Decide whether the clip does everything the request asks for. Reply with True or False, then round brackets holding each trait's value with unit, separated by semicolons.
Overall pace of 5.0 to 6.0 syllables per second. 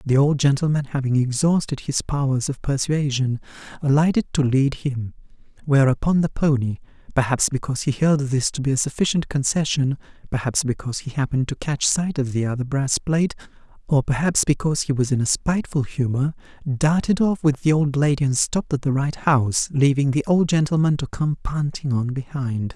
True (5.5 syllables/s)